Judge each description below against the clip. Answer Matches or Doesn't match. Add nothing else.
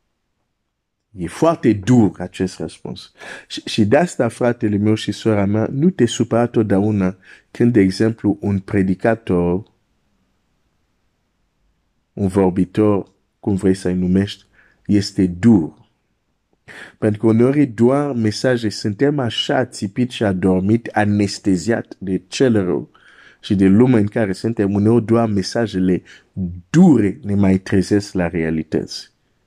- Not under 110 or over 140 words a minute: Matches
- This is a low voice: Matches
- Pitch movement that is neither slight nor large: Matches